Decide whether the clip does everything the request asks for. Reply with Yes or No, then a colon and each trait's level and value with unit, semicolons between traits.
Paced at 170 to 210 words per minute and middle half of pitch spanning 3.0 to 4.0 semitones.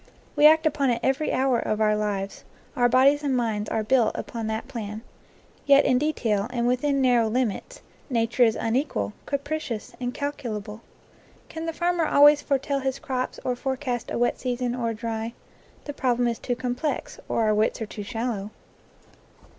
Yes: average, 175 wpm; average, 3.6 semitones